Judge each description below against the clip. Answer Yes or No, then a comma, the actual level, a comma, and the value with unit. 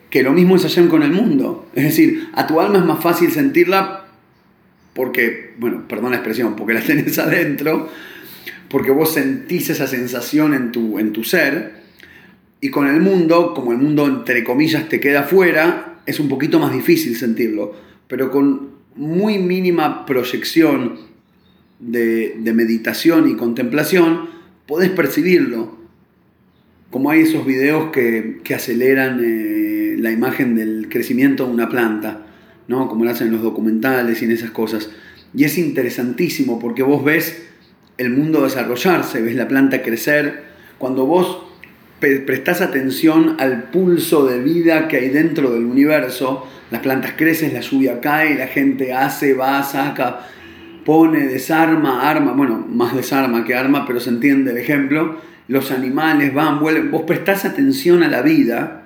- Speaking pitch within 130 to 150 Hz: Yes, medium, 140 Hz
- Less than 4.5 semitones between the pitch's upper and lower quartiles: No, wide, 5.4 semitones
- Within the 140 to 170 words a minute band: Yes, average, 155 wpm